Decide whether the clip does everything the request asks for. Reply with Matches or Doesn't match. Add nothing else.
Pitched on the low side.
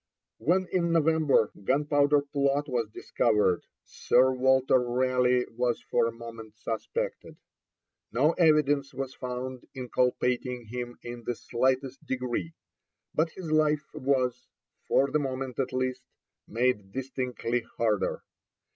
Matches